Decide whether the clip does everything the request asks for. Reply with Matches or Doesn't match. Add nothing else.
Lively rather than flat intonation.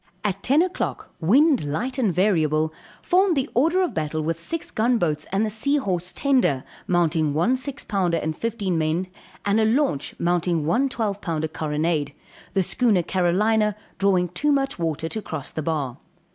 Matches